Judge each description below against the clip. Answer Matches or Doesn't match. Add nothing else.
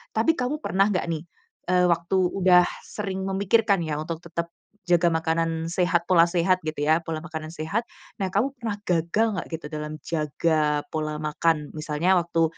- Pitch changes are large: Doesn't match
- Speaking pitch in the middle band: Matches